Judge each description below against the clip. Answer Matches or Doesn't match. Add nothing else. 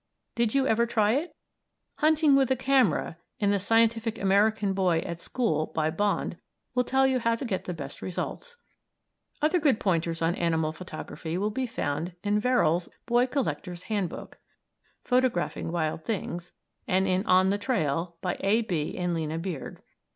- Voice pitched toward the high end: Matches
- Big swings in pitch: Matches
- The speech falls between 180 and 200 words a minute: Doesn't match